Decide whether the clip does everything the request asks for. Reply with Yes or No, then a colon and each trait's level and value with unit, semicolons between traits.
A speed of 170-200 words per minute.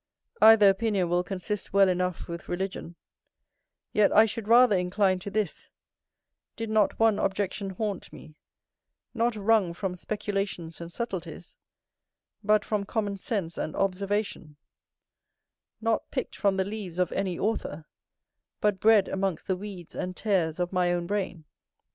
No: average, 140 wpm